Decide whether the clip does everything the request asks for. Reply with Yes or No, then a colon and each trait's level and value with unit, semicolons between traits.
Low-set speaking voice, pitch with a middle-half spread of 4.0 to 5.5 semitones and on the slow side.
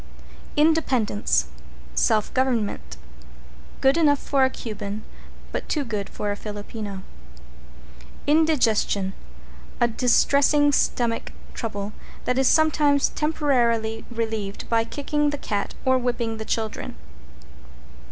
No: high, 235 Hz; average, 5.1 semitones; slow, 105 wpm